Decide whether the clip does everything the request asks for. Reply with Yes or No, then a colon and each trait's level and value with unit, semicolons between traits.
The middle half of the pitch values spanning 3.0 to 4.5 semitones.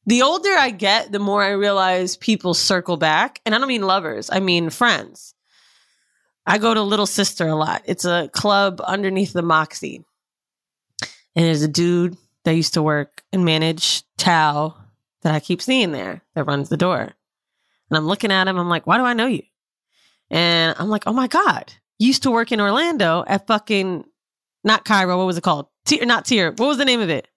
No: average, 5.0 semitones